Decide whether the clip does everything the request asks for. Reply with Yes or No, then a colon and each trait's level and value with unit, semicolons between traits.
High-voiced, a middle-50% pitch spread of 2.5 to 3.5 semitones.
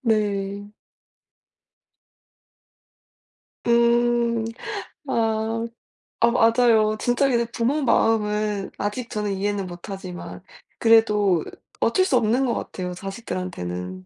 Yes: high, 220 Hz; average, 3.1 semitones